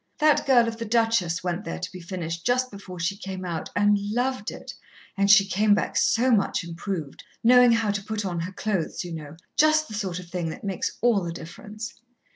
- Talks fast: Yes, fast, 215 wpm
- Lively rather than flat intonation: No, average, 4.5 semitones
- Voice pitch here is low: No, high, 200 Hz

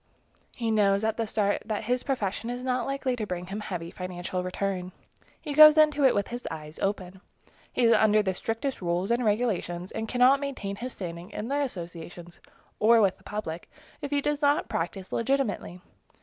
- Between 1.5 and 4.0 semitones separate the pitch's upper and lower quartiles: No, wide, 5.4 semitones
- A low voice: No, high, 215 Hz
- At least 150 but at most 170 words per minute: No, average, 190 wpm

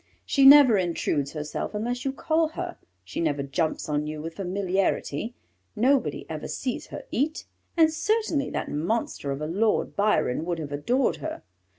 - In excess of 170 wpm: No, average, 165 wpm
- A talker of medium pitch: No, high, 200 Hz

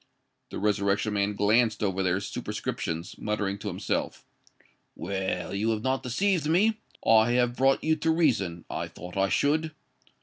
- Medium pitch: No, low, 110 Hz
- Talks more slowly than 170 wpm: Yes, average, 145 wpm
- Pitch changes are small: No, wide, 5.4 semitones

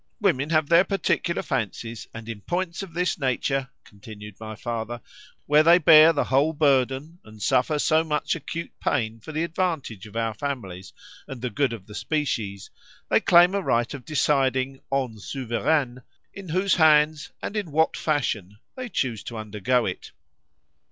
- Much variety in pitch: Yes, wide, 5.8 semitones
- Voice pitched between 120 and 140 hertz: Yes, low, 135 Hz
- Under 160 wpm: No, average, 165 wpm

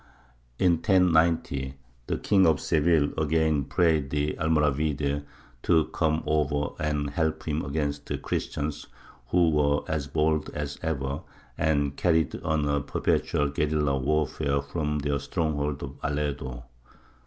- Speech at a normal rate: No, slow, 130 wpm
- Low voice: Yes, very low, 75 Hz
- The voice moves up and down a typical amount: No, narrow, 1.7 semitones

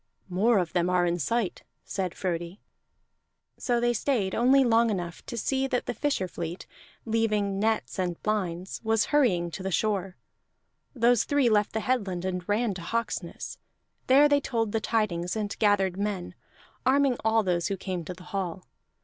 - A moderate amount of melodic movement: Yes, average, 4.3 semitones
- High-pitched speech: Yes, high, 205 Hz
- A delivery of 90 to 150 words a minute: No, average, 170 wpm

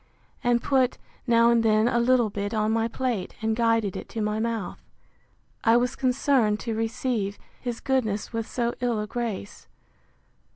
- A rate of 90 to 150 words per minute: No, average, 165 wpm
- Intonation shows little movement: Yes, narrow, 2.0 semitones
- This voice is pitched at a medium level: No, high, 230 Hz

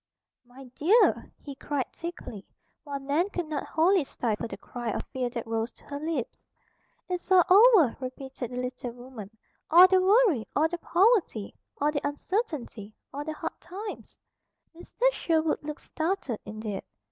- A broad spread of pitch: Yes, wide, 6.2 semitones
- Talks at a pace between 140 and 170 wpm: Yes, average, 160 wpm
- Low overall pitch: No, very high, 290 Hz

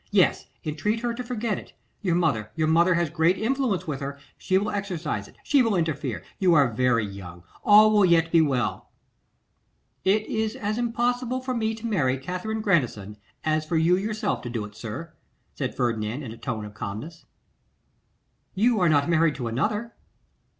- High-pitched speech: No, medium, 170 Hz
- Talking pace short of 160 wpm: No, average, 180 wpm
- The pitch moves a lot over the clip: Yes, wide, 8.6 semitones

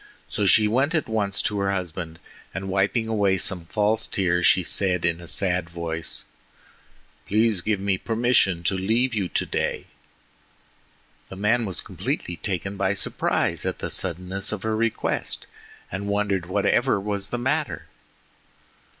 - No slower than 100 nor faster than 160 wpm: Yes, average, 150 wpm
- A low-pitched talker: Yes, low, 100 Hz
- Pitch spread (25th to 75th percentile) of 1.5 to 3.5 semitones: Yes, average, 2.9 semitones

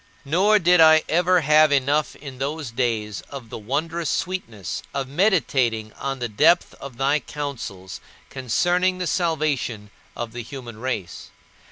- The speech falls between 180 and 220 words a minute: No, average, 145 wpm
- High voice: No, medium, 140 Hz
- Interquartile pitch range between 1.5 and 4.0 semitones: No, wide, 5.6 semitones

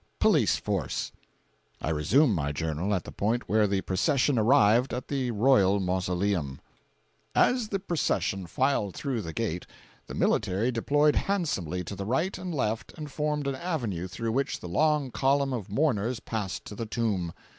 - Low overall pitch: Yes, low, 115 Hz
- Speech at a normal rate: Yes, average, 165 wpm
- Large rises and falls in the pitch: Yes, wide, 6.8 semitones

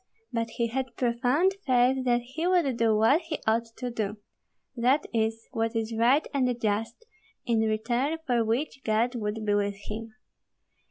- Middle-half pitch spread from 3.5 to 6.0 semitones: No, narrow, 2.6 semitones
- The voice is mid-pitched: No, high, 235 Hz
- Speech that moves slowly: No, average, 165 wpm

